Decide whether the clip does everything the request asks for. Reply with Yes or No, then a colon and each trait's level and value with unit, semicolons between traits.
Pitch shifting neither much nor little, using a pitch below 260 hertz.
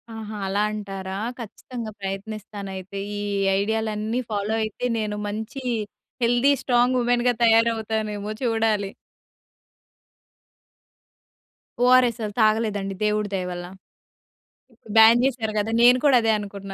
No: narrow, 2.3 semitones; high, 215 Hz